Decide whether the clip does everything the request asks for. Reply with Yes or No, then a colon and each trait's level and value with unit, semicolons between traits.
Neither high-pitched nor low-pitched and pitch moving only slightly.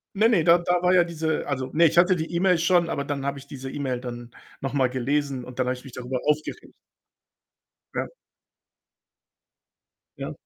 No: medium, 145 Hz; average, 4.7 semitones